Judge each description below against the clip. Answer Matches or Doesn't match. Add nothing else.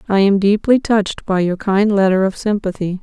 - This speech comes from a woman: Matches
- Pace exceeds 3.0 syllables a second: Matches